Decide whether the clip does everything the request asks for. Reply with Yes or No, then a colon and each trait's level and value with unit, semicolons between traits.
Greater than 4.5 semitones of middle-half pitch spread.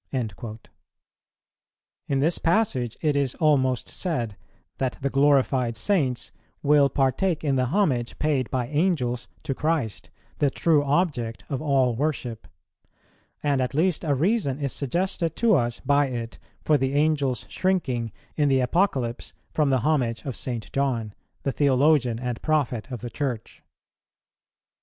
No: average, 3.6 semitones